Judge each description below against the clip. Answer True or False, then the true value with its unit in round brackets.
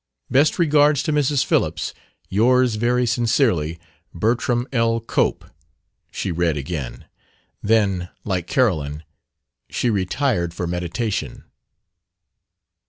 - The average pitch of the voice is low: True (110 Hz)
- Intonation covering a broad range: True (6.3 semitones)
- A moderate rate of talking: False (100 wpm)